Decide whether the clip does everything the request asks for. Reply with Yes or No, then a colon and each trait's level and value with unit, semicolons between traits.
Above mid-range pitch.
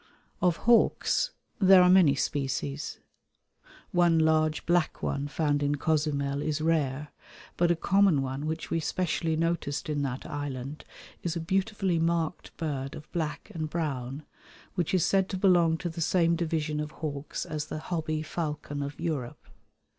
No: medium, 155 Hz